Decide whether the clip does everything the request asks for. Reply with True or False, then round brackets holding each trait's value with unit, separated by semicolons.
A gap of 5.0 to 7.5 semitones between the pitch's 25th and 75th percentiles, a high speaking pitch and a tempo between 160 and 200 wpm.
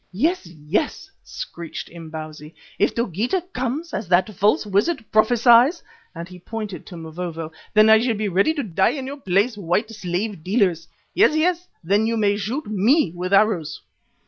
True (5.5 semitones; 210 Hz; 165 wpm)